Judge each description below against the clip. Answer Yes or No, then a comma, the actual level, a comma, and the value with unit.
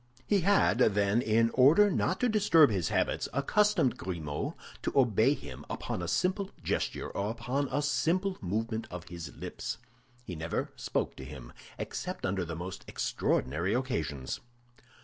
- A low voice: Yes, low, 110 Hz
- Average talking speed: Yes, average, 150 wpm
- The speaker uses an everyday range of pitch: No, wide, 9.0 semitones